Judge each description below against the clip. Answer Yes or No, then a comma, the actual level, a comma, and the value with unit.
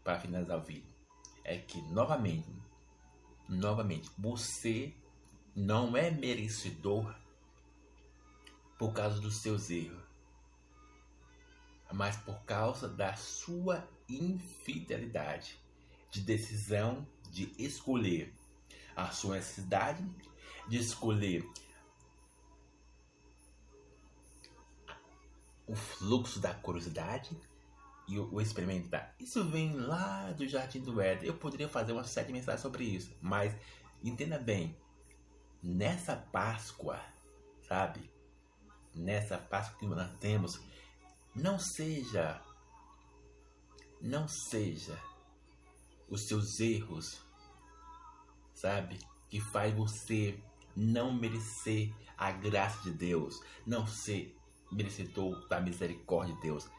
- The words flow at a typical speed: No, slow, 95 wpm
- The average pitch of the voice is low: Yes, low, 100 Hz